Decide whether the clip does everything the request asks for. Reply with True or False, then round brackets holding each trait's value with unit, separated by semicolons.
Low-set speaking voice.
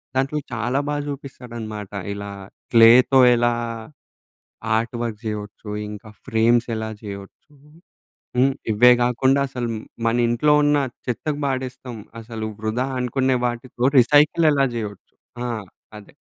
True (120 Hz)